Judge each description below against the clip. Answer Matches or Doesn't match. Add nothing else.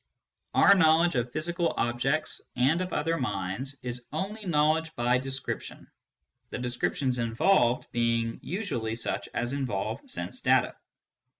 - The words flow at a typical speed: Doesn't match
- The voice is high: Doesn't match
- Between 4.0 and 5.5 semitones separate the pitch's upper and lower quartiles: Matches